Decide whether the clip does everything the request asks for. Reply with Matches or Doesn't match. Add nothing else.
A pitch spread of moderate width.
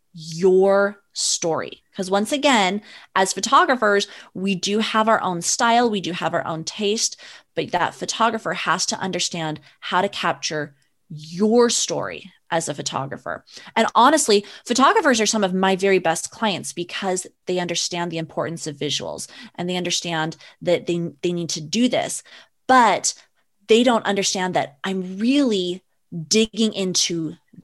Matches